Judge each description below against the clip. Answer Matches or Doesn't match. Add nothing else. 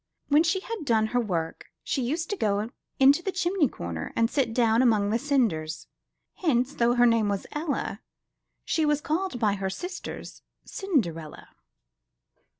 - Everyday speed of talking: Matches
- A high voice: Matches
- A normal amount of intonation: Doesn't match